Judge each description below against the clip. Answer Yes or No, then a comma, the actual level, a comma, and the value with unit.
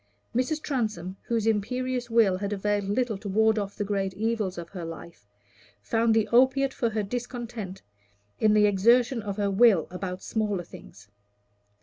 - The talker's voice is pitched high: Yes, high, 215 Hz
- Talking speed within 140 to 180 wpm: Yes, average, 160 wpm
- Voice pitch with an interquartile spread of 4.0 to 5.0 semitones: No, average, 3.3 semitones